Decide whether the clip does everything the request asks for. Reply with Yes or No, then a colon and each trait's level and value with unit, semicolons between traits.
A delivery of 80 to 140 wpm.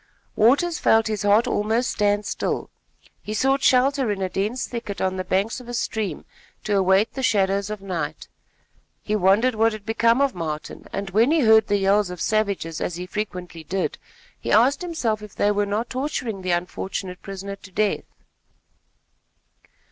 No: average, 175 wpm